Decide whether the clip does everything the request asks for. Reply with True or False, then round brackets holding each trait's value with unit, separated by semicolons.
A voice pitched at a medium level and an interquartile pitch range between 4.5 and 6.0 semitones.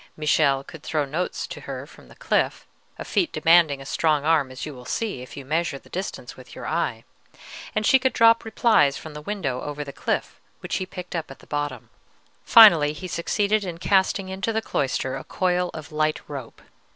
True (155 Hz; 4.9 semitones)